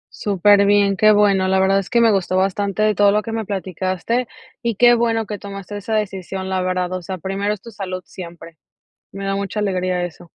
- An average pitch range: No, narrow, 2.0 semitones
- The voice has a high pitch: Yes, high, 195 Hz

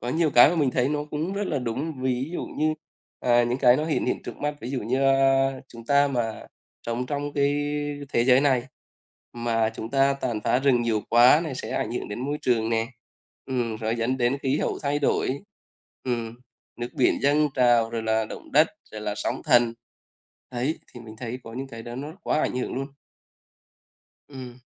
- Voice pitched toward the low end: Yes, low, 125 Hz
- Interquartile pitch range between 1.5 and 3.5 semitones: Yes, average, 3.2 semitones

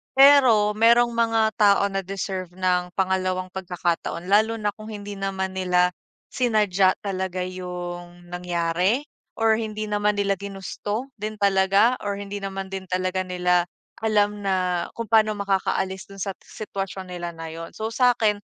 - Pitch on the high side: Yes, high, 195 Hz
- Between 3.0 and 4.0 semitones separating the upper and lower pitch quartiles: No, narrow, 2.6 semitones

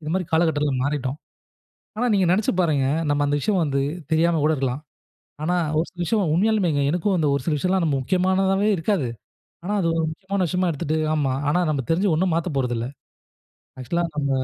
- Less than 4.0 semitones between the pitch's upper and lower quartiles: No, average, 4.3 semitones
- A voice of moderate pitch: Yes, medium, 165 Hz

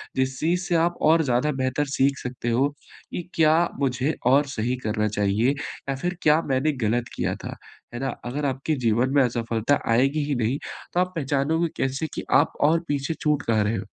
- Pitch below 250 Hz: Yes, low, 135 Hz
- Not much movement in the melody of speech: No, average, 3.8 semitones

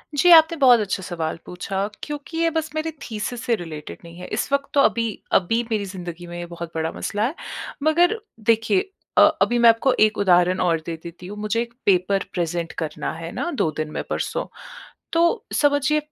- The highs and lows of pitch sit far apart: Yes, wide, 8.2 semitones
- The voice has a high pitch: Yes, high, 210 Hz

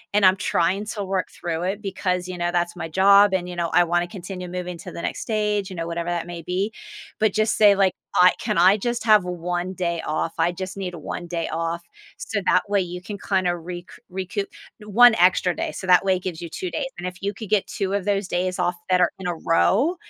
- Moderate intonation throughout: No, narrow, 2.3 semitones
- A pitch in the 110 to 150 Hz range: No, medium, 185 Hz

